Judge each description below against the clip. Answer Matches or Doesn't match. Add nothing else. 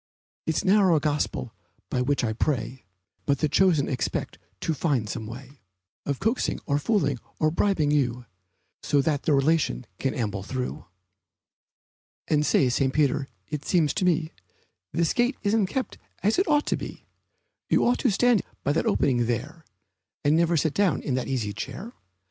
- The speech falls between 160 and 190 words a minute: Matches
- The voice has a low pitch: Doesn't match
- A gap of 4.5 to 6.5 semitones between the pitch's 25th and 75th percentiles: Matches